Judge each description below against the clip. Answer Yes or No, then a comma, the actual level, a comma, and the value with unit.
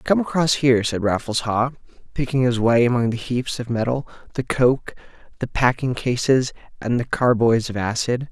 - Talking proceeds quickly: No, average, 175 wpm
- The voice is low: Yes, low, 125 Hz